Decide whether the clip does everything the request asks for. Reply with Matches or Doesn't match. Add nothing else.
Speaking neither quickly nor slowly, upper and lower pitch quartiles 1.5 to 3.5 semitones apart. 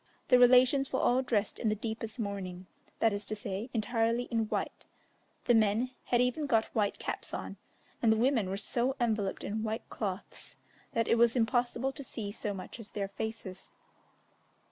Matches